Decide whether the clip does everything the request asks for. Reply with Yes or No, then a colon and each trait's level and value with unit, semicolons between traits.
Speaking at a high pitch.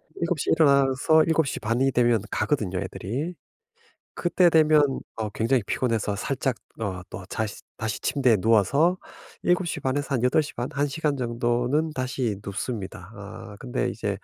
No: low, 125 Hz